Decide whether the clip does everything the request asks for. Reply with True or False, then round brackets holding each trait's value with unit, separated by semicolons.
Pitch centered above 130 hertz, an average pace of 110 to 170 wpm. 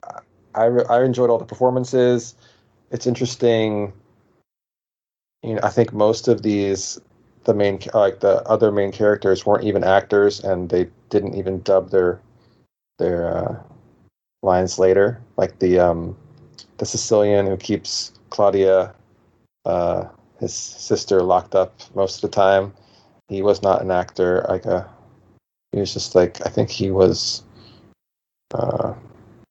False (105 Hz; 140 wpm)